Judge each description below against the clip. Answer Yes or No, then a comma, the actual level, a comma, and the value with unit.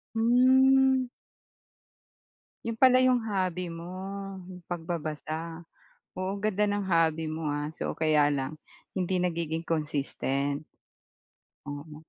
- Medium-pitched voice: Yes, medium, 170 Hz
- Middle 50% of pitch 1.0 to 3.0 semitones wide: No, average, 4.8 semitones